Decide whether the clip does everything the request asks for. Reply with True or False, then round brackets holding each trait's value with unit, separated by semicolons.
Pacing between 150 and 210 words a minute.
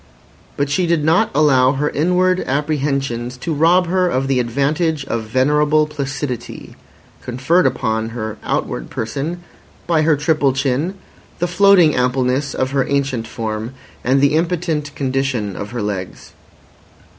False (140 wpm)